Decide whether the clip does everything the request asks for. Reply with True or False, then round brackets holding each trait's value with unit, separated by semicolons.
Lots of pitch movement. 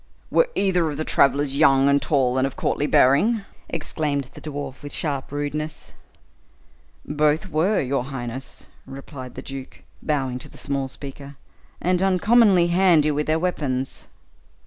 False (3.2 semitones)